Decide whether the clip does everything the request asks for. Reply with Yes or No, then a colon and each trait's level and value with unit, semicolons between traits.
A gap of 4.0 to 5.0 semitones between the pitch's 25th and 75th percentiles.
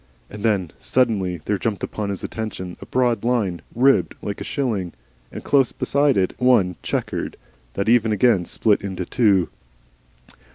Yes: average, 4.4 semitones